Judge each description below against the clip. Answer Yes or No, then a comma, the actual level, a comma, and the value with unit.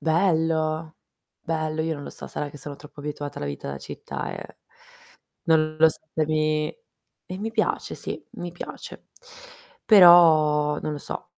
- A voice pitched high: No, medium, 155 Hz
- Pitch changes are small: Yes, narrow, 1.7 semitones